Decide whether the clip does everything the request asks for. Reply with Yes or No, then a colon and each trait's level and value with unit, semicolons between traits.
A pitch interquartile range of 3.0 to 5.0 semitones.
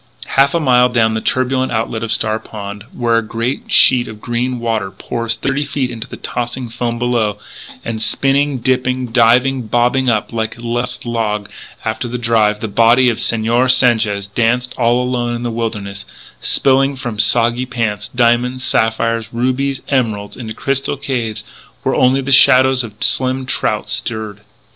No: narrow, 2.4 semitones